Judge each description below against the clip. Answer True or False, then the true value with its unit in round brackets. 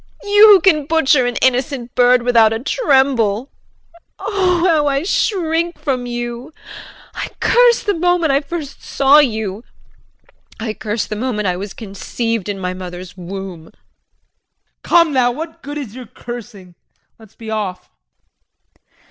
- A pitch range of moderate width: False (6.6 semitones)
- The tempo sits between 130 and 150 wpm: True (145 wpm)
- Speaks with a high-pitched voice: True (250 Hz)